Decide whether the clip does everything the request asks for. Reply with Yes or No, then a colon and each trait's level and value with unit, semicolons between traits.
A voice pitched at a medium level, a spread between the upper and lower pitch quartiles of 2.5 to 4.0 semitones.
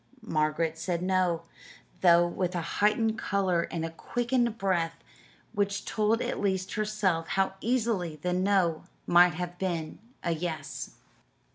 Yes: medium, 180 Hz; average, 3.3 semitones